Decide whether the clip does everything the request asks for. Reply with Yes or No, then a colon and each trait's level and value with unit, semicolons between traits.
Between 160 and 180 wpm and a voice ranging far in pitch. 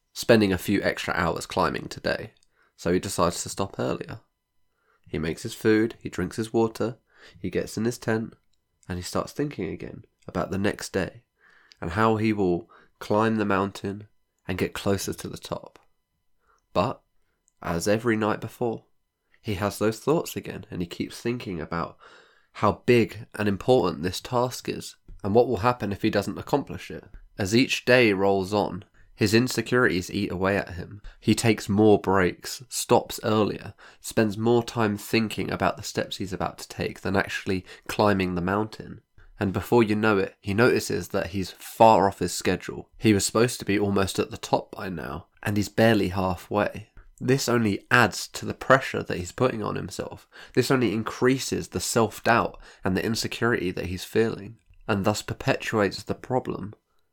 No: average, 175 wpm; average, 3.0 semitones